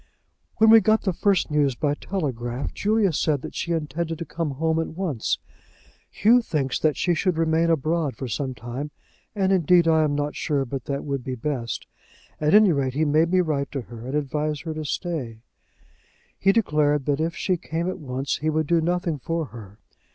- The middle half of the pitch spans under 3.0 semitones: No, average, 3.6 semitones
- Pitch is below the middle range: No, medium, 155 Hz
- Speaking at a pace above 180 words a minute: Yes, average, 200 wpm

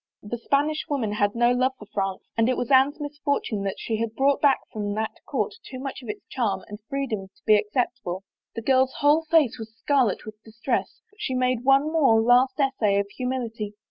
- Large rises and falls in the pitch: No, average, 4.1 semitones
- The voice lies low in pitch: No, high, 245 Hz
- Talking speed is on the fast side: Yes, fast, 210 wpm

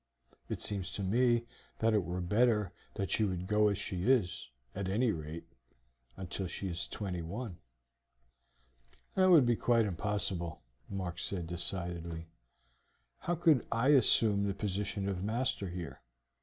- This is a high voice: No, low, 100 Hz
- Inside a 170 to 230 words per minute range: No, average, 145 wpm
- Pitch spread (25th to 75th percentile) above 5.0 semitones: No, average, 4.2 semitones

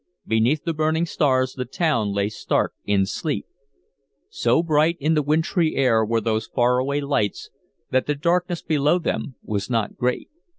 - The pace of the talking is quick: No, average, 165 wpm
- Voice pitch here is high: No, medium, 140 Hz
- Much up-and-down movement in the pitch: Yes, wide, 5.8 semitones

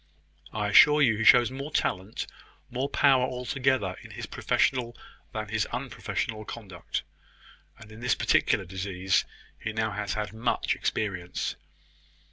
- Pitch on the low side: Yes, low, 110 Hz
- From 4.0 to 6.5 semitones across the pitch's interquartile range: No, average, 3.6 semitones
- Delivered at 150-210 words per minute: No, slow, 135 wpm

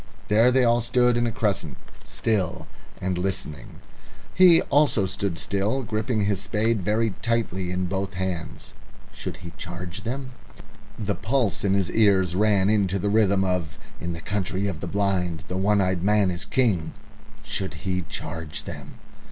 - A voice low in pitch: Yes, low, 100 Hz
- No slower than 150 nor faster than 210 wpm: Yes, average, 160 wpm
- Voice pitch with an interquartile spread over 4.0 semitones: No, average, 3.2 semitones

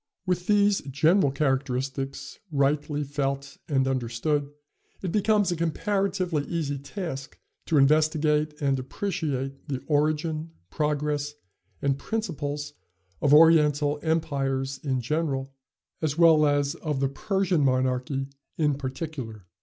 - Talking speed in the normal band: No, slow, 115 wpm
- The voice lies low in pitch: No, medium, 145 Hz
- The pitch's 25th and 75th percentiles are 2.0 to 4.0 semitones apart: Yes, average, 2.9 semitones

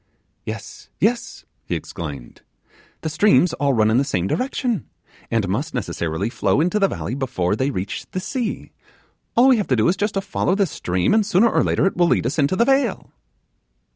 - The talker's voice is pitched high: No, medium, 155 Hz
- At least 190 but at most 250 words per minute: Yes, average, 200 wpm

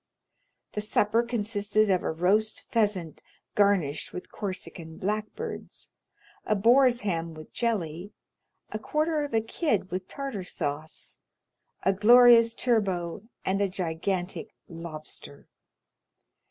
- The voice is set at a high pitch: Yes, high, 205 Hz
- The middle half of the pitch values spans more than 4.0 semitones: Yes, average, 4.4 semitones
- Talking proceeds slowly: Yes, slow, 115 wpm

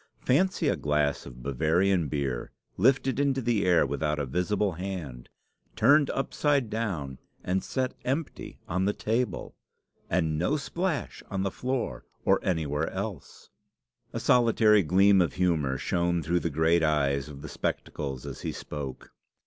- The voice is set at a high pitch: No, very low, 90 Hz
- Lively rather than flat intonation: Yes, wide, 7.2 semitones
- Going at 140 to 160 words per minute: Yes, average, 150 wpm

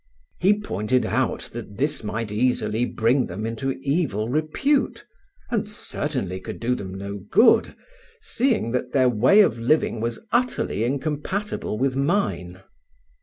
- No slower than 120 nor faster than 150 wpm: Yes, slow, 135 wpm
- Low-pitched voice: Yes, low, 125 Hz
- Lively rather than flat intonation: Yes, wide, 6.2 semitones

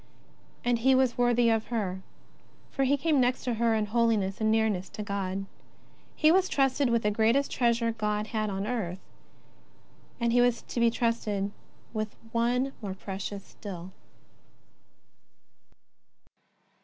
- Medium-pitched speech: No, high, 230 Hz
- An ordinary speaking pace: Yes, average, 145 wpm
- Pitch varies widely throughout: No, average, 2.9 semitones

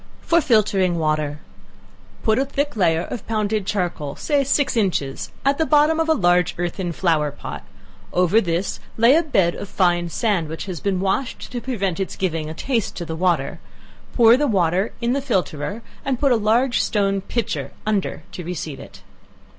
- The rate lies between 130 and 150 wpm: No, average, 180 wpm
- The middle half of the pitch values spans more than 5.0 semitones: Yes, wide, 5.6 semitones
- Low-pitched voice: No, high, 195 Hz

